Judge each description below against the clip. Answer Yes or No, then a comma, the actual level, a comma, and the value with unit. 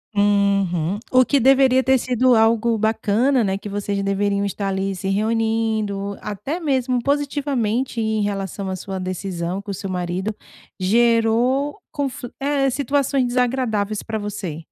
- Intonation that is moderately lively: Yes, average, 4.3 semitones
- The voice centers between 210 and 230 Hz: Yes, high, 220 Hz